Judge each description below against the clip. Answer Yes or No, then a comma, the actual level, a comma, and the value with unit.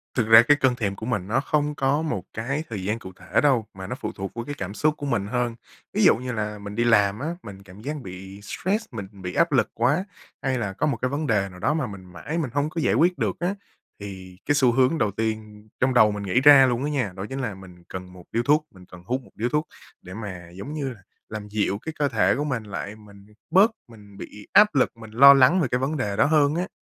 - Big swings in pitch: Yes, wide, 6.0 semitones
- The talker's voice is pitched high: No, low, 115 Hz